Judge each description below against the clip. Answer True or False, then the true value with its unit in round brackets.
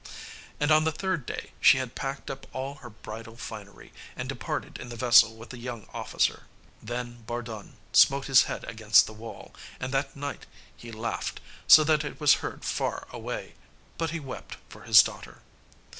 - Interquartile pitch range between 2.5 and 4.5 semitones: True (3.7 semitones)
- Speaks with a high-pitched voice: False (125 Hz)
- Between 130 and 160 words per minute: False (180 wpm)